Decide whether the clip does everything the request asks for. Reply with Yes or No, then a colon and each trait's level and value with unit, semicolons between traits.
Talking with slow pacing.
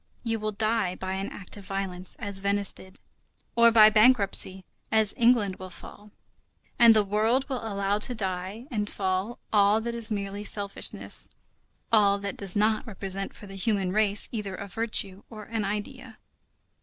No: average, 170 wpm